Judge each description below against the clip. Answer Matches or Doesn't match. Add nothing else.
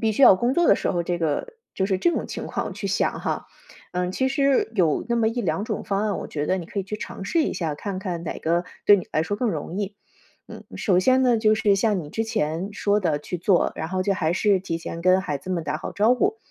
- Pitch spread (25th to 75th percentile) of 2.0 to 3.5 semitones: Doesn't match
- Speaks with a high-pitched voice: Matches